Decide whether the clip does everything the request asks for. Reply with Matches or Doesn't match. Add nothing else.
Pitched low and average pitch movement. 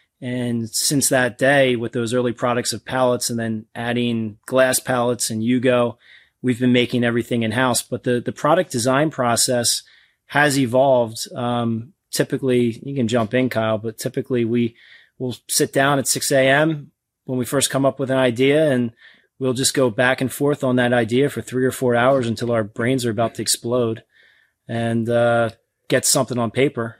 Doesn't match